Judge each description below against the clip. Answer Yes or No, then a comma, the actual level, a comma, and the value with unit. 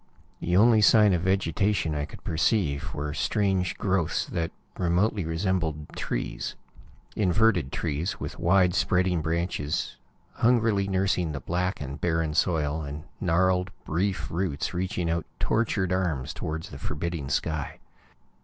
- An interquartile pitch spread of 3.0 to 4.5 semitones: Yes, average, 3.4 semitones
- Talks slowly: Yes, slow, 130 wpm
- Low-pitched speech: Yes, very low, 90 Hz